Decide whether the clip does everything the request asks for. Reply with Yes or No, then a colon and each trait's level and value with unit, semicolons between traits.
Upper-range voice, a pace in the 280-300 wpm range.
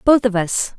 No: high, 225 Hz; fast, 230 wpm